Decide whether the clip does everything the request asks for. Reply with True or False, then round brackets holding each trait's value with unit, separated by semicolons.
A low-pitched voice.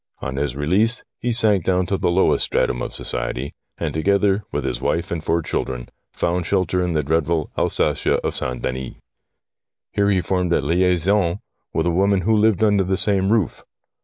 True (90 Hz)